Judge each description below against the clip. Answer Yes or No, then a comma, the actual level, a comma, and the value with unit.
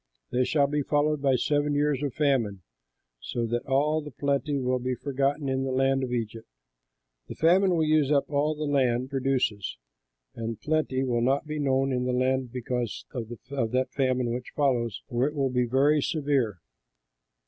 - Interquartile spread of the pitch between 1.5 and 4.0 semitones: Yes, average, 2.7 semitones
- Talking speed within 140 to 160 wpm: No, average, 180 wpm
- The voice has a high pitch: No, low, 135 Hz